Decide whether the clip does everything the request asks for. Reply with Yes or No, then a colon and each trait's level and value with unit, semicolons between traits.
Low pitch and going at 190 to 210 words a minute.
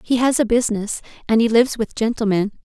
No: high, 225 Hz; fast, 205 wpm